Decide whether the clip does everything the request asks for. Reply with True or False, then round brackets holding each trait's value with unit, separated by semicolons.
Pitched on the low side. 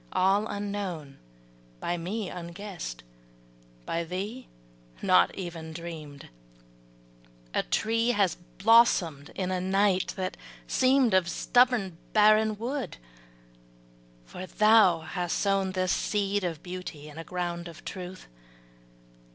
False (185 Hz)